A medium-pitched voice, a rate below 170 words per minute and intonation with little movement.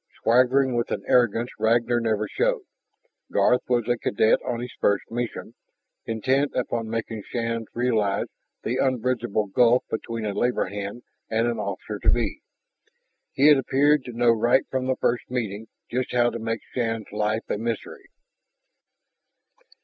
No: low, 120 Hz; average, 150 wpm; narrow, 2.0 semitones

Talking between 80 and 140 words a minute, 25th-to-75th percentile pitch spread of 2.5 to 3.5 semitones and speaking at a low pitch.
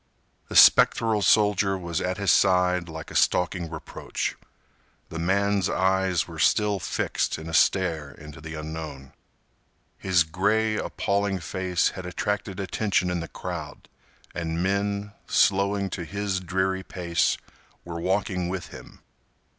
Yes: slow, 135 wpm; average, 2.9 semitones; very low, 95 Hz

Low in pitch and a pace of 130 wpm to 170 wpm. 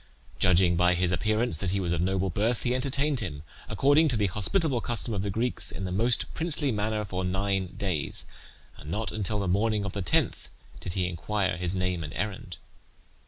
No: low, 100 Hz; average, 200 wpm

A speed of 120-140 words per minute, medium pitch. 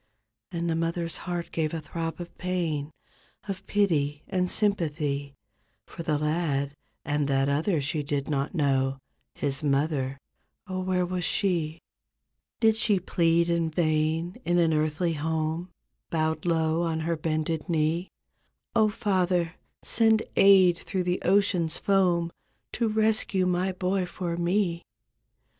Yes: slow, 135 wpm; medium, 170 Hz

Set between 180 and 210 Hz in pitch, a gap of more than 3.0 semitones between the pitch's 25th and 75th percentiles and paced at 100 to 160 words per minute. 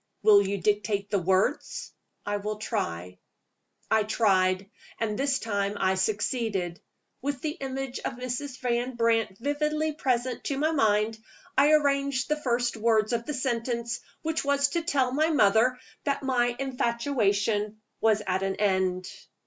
No: high, 235 Hz; average, 4.8 semitones; average, 150 wpm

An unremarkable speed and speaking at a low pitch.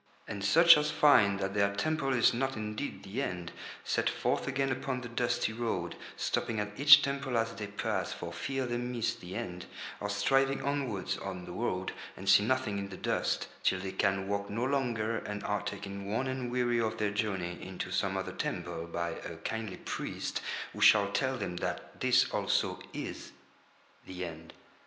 Yes: average, 185 wpm; low, 105 Hz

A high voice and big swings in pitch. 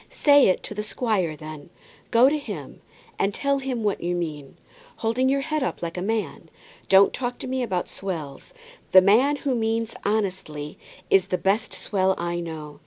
Yes: high, 200 Hz; wide, 6.1 semitones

